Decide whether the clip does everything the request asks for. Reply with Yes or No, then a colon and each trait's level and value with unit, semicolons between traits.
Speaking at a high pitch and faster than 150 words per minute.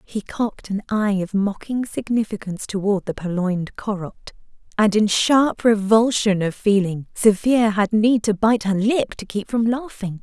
Yes: high, 210 Hz; average, 165 wpm